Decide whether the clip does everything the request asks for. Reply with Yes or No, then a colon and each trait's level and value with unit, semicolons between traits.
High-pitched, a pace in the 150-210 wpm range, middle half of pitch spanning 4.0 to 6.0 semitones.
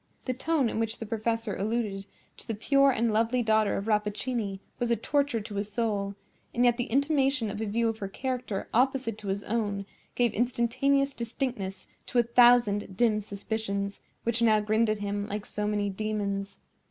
No: high, 225 Hz; average, 185 wpm; average, 2.8 semitones